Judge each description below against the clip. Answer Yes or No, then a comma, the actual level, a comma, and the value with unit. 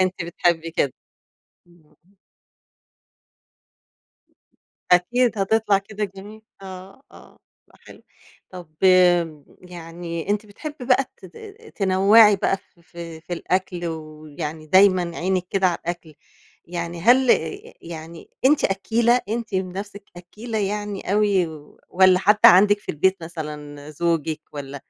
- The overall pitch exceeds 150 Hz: Yes, medium, 185 Hz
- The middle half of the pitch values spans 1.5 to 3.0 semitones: No, average, 3.5 semitones